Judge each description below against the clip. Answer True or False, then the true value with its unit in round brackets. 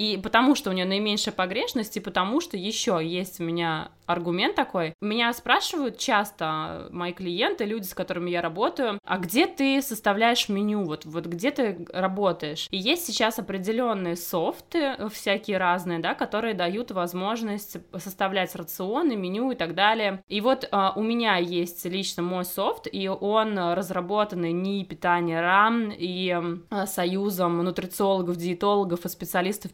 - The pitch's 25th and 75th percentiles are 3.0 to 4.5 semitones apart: True (3.6 semitones)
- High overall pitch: True (195 Hz)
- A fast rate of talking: False (150 wpm)